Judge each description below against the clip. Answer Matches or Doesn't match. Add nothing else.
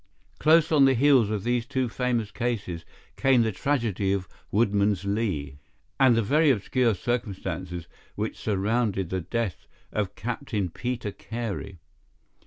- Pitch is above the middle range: Doesn't match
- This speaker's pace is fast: Doesn't match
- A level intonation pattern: Doesn't match